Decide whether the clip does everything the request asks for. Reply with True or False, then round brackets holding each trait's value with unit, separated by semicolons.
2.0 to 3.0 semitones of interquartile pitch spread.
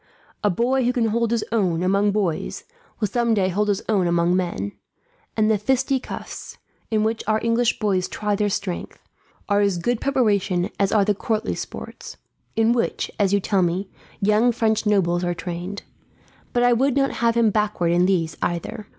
False (3.7 semitones)